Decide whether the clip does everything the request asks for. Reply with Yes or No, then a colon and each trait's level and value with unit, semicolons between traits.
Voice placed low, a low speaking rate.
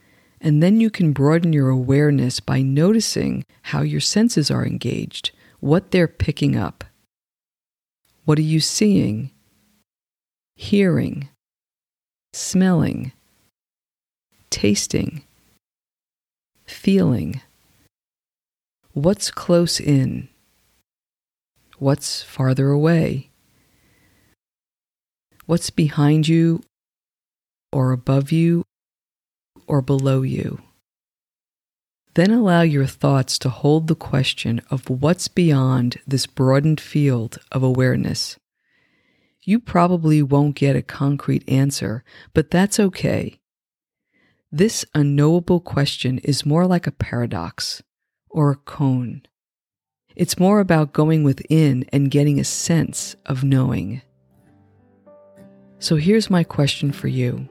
No: medium, 145 Hz; slow, 100 wpm